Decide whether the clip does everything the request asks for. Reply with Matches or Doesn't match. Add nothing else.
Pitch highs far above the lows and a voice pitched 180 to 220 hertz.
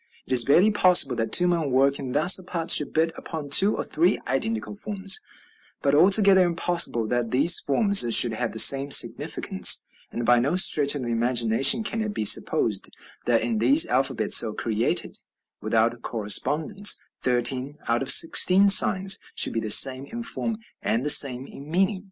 Doesn't match